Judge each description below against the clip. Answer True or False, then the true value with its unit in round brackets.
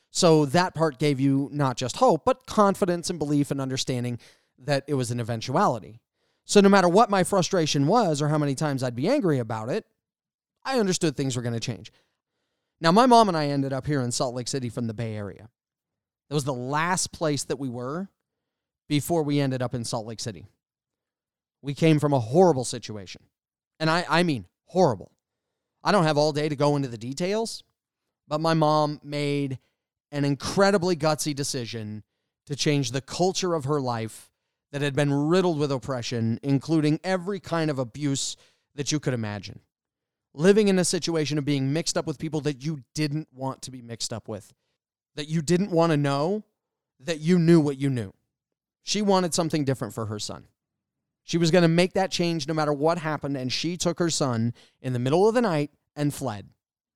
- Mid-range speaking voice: True (150 Hz)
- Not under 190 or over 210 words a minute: True (195 wpm)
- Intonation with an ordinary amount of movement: True (4.4 semitones)